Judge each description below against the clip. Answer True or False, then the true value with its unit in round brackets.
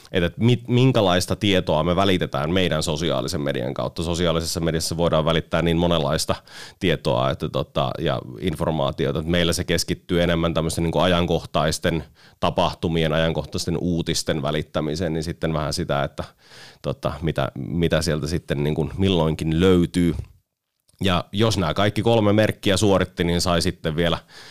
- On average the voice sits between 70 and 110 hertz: True (85 Hz)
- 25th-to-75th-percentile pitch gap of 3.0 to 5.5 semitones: False (2.5 semitones)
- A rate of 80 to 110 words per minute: False (140 wpm)